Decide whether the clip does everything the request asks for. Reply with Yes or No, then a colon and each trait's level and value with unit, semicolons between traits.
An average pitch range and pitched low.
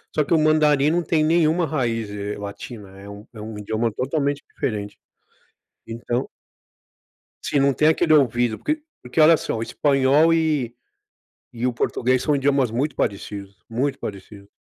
No: wide, 5.8 semitones; low, 130 Hz